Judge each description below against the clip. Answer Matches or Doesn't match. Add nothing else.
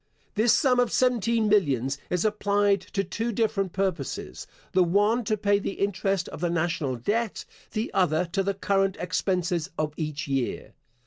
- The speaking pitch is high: Matches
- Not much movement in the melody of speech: Doesn't match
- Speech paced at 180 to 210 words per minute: Doesn't match